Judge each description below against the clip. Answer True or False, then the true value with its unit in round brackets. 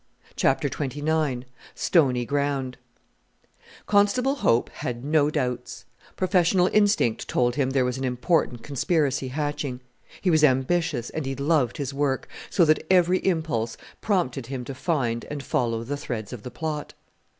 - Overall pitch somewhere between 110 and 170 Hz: True (140 Hz)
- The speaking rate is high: False (145 wpm)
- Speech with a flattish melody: False (4.4 semitones)